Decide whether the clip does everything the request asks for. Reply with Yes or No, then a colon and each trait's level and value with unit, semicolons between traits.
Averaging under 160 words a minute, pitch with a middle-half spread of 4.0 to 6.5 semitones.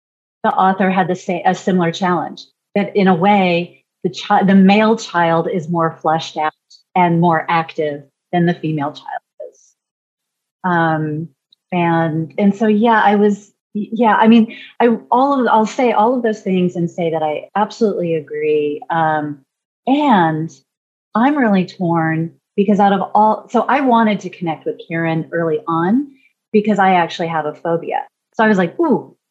No: average, 170 wpm; average, 4.5 semitones